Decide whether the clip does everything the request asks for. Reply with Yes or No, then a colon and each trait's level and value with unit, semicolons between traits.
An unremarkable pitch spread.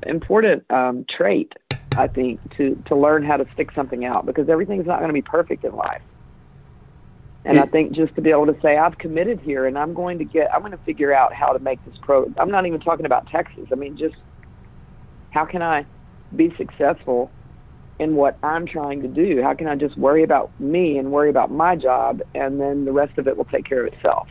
Yes: average, 3.3 semitones